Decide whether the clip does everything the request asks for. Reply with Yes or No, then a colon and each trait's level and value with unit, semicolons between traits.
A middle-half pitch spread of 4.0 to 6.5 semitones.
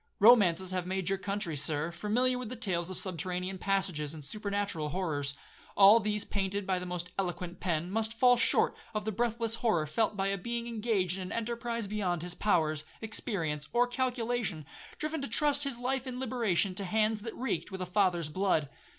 Yes: average, 4.6 semitones